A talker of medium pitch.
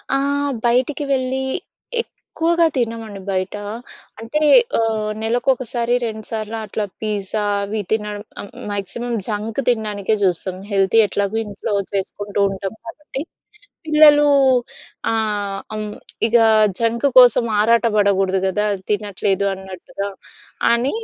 No: high, 220 Hz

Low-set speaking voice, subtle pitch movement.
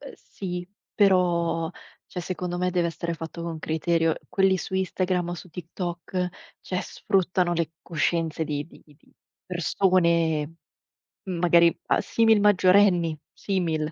No: medium, 175 Hz; narrow, 1.9 semitones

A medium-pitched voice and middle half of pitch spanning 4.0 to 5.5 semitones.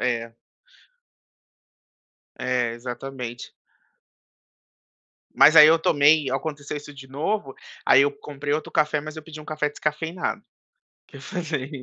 No: medium, 145 Hz; average, 2.7 semitones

